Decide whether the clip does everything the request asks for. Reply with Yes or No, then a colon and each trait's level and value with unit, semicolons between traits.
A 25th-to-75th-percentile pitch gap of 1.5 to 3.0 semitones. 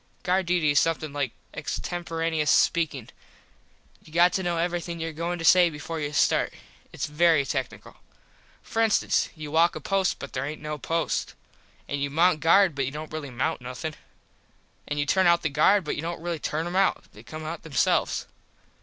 Yes: average, 2.7 semitones